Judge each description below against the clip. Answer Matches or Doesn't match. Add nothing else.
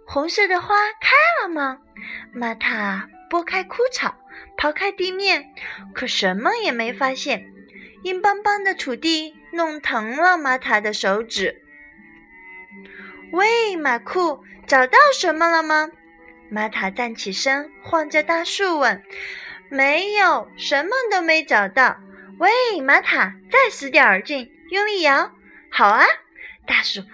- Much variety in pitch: Matches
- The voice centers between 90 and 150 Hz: Doesn't match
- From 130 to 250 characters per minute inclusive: Matches